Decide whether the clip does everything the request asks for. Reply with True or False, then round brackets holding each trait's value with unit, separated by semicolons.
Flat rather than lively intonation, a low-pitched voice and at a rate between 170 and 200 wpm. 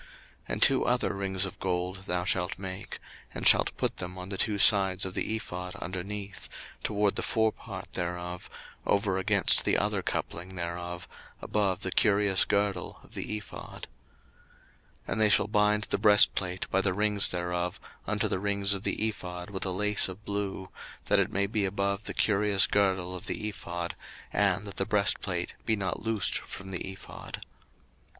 True (2.1 semitones; 95 Hz; 175 wpm)